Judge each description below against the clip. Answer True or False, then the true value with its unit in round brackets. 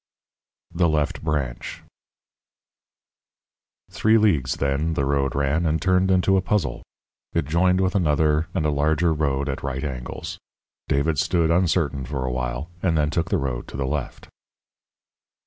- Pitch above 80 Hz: False (75 Hz)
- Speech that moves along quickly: False (150 wpm)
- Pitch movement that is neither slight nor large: True (3.7 semitones)